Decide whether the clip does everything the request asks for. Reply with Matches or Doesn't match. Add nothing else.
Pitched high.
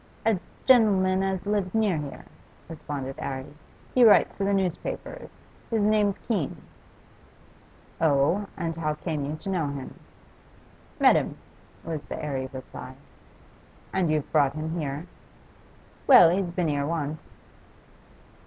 Doesn't match